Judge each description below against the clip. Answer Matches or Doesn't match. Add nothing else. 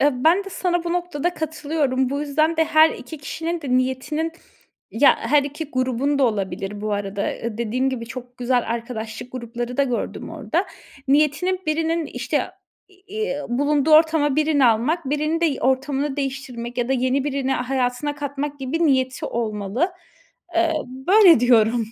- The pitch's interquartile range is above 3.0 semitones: Matches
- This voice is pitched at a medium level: Doesn't match